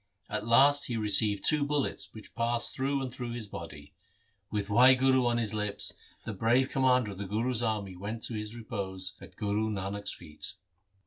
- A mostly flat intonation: No, average, 3.7 semitones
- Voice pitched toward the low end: Yes, low, 110 Hz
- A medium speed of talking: Yes, average, 180 wpm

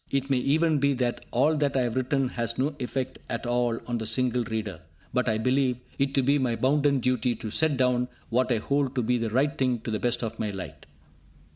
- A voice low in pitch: Yes, low, 125 Hz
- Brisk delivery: Yes, fast, 235 wpm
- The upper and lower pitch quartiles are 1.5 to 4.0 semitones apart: Yes, narrow, 2.6 semitones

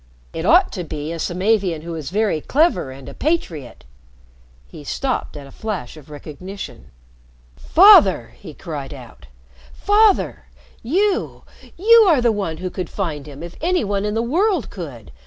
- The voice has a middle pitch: Yes, medium, 180 Hz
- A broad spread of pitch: Yes, wide, 9.0 semitones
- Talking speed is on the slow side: No, average, 165 wpm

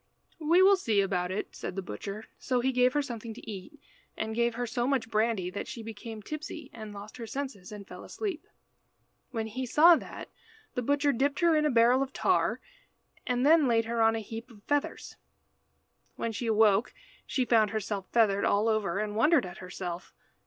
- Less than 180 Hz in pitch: No, high, 230 Hz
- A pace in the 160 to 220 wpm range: Yes, average, 195 wpm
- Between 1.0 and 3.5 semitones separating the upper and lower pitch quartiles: No, average, 4.1 semitones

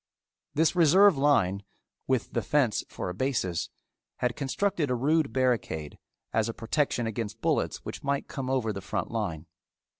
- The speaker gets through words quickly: No, average, 155 wpm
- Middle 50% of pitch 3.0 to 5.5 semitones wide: Yes, average, 4.9 semitones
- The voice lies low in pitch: Yes, low, 125 Hz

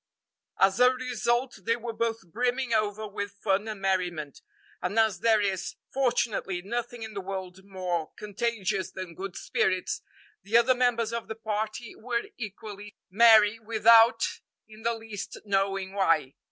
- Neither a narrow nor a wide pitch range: Yes, average, 3.1 semitones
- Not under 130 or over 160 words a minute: Yes, average, 150 wpm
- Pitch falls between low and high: No, high, 215 Hz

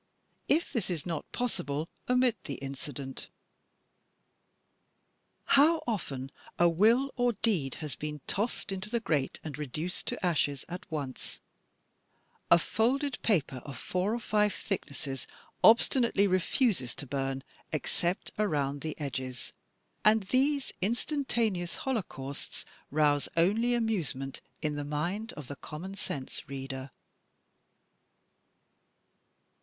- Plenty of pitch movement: Yes, wide, 7.9 semitones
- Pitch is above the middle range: No, medium, 175 Hz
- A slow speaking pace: Yes, slow, 115 wpm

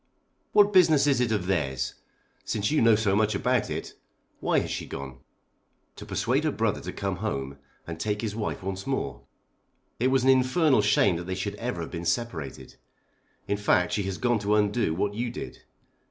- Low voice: Yes, low, 105 Hz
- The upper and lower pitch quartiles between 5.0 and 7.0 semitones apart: Yes, average, 5.3 semitones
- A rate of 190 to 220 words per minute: Yes, average, 195 wpm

